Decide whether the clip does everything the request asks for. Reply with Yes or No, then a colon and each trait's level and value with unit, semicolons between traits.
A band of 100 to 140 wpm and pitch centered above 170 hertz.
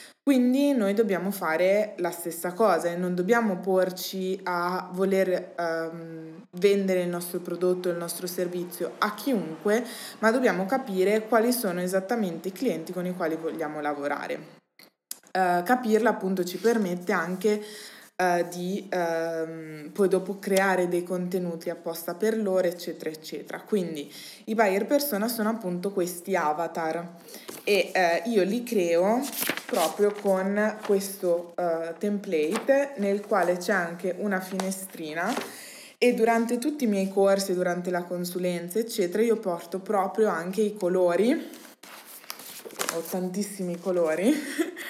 Yes: average, 130 wpm; high, 190 Hz